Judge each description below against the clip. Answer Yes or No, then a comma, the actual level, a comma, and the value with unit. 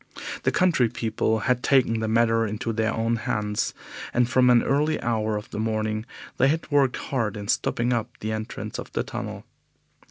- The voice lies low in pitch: Yes, low, 115 Hz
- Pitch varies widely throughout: No, narrow, 2.4 semitones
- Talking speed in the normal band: Yes, average, 185 wpm